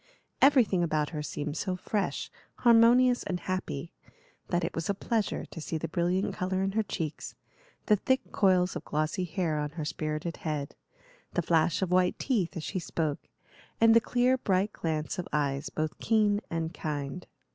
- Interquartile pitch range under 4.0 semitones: No, average, 4.6 semitones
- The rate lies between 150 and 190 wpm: Yes, average, 175 wpm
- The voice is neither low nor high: Yes, medium, 180 Hz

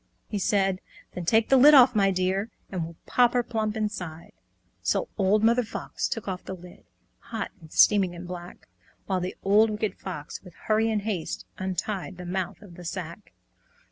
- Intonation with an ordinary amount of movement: Yes, average, 3.3 semitones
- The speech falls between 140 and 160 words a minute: No, average, 185 wpm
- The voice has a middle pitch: No, high, 195 Hz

